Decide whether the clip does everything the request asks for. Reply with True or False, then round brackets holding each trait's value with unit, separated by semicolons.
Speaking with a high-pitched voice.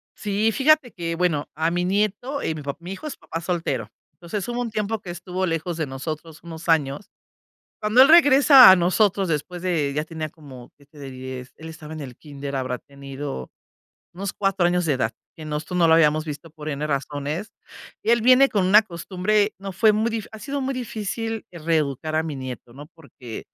False (170 Hz)